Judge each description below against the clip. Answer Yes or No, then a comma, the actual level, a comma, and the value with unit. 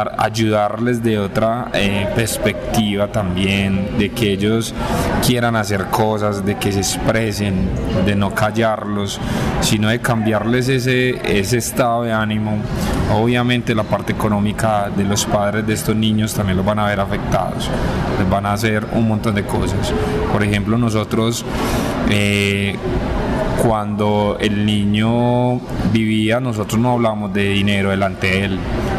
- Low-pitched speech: Yes, low, 105 Hz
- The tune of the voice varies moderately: No, narrow, 2.0 semitones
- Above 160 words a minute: No, average, 140 wpm